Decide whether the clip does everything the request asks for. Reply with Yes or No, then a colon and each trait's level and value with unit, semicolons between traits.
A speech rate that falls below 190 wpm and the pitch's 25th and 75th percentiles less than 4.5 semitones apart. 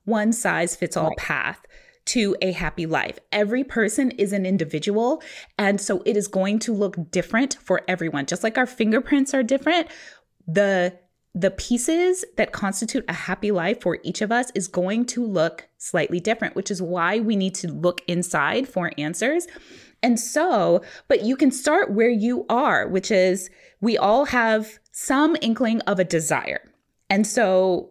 No: average, 170 wpm; average, 5.1 semitones